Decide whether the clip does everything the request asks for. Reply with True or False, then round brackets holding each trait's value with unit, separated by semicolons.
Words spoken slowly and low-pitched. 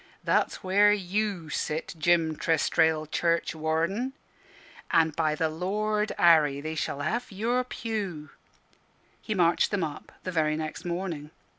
False (130 wpm; 170 Hz)